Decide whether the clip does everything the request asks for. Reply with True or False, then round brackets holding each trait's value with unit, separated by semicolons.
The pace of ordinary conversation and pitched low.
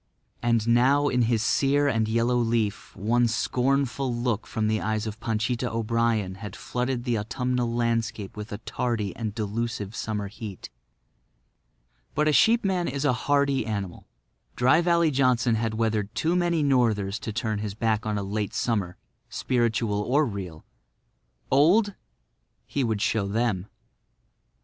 True (145 wpm; 115 Hz)